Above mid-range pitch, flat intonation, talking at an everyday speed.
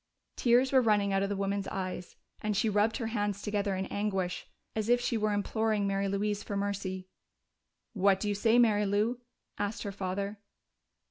Yes: high, 205 Hz; narrow, 1.6 semitones; average, 185 wpm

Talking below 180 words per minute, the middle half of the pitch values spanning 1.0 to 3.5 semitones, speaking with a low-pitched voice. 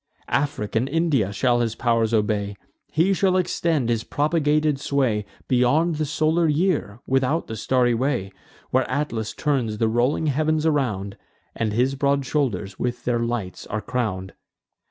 No: average, 150 wpm; average, 5.0 semitones; low, 125 Hz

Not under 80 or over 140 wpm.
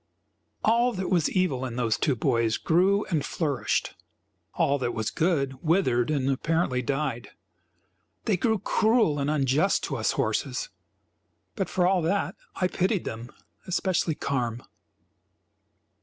Yes: slow, 135 wpm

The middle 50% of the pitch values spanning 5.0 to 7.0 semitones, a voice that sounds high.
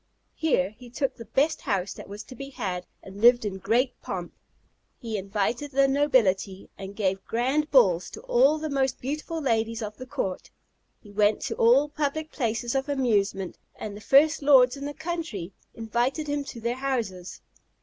Yes: wide, 5.5 semitones; high, 245 Hz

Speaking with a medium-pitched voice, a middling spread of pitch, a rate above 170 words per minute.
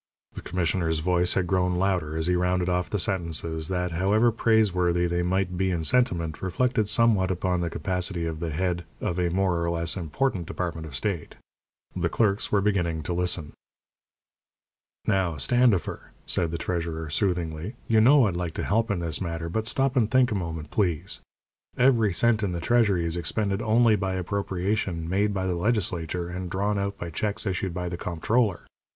No: very low, 90 Hz; average, 3.3 semitones; average, 180 wpm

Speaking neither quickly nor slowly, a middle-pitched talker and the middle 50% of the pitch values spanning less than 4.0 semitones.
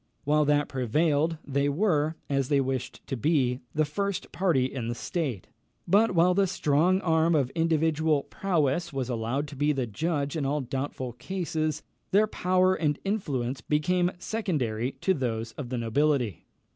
No: average, 160 wpm; medium, 150 Hz; average, 4.4 semitones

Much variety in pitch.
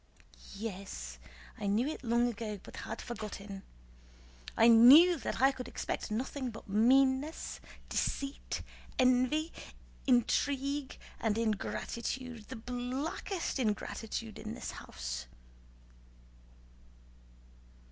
No: average, 3.7 semitones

